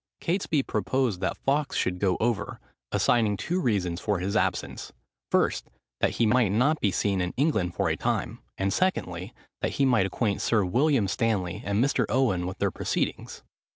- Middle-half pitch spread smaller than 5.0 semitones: No, wide, 5.6 semitones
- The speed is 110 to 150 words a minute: No, average, 175 wpm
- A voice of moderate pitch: No, low, 105 Hz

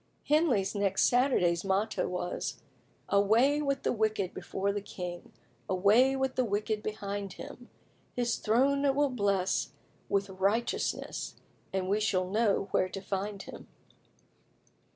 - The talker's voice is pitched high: Yes, high, 205 Hz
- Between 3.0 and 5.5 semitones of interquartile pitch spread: Yes, average, 4.1 semitones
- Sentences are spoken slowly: Yes, slow, 130 wpm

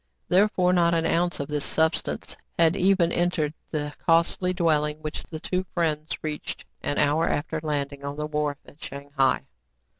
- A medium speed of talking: Yes, average, 170 wpm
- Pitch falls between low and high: Yes, medium, 155 Hz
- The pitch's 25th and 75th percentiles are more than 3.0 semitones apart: No, narrow, 2.6 semitones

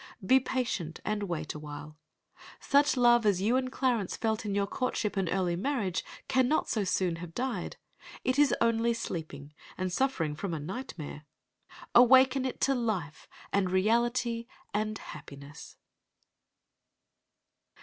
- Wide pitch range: Yes, wide, 6.1 semitones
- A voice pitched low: No, high, 215 Hz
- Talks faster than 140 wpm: No, slow, 135 wpm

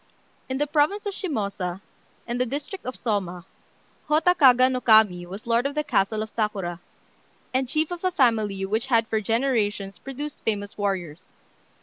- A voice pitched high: Yes, high, 230 Hz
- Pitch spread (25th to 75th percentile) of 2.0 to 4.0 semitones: No, wide, 5.5 semitones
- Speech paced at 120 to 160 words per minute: No, average, 170 wpm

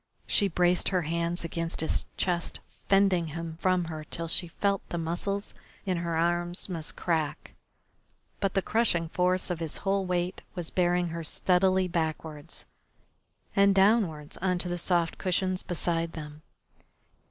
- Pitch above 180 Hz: No, medium, 175 Hz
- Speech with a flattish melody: Yes, narrow, 2.1 semitones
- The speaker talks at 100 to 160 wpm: Yes, average, 150 wpm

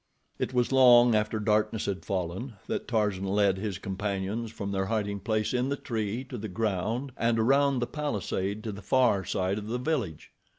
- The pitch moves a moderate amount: Yes, average, 3.6 semitones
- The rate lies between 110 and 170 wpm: No, average, 185 wpm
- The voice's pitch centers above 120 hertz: No, low, 110 Hz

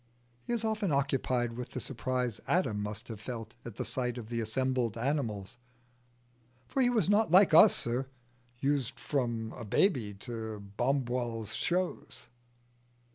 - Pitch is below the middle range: Yes, low, 125 Hz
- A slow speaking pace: No, average, 145 wpm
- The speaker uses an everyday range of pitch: Yes, average, 3.8 semitones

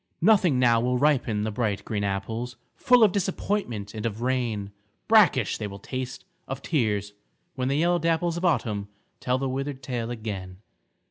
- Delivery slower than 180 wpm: Yes, average, 165 wpm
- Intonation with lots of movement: Yes, wide, 5.9 semitones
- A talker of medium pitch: No, low, 125 Hz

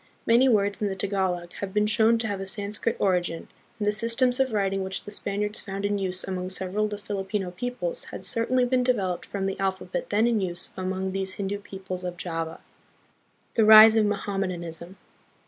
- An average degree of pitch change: No, narrow, 2.3 semitones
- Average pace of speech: Yes, average, 195 wpm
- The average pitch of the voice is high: Yes, high, 200 Hz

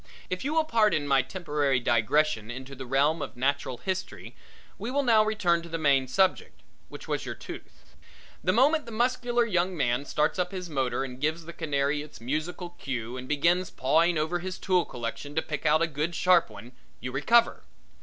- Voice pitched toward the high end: No, medium, 155 Hz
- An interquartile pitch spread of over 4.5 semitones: Yes, average, 5.3 semitones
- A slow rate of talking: No, average, 195 wpm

